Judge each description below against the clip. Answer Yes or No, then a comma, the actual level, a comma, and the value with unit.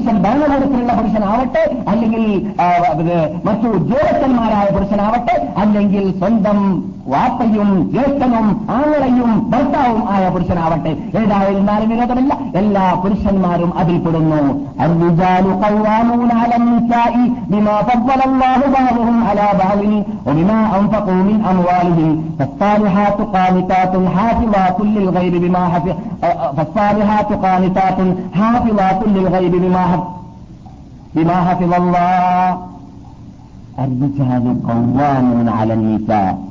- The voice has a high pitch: Yes, high, 200 Hz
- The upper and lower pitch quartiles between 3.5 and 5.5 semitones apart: Yes, average, 4.0 semitones